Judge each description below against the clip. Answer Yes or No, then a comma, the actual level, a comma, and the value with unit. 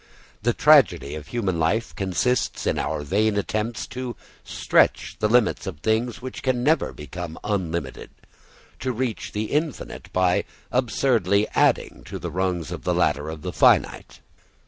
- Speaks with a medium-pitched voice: No, low, 105 Hz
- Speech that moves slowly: No, average, 150 wpm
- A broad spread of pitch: Yes, wide, 5.8 semitones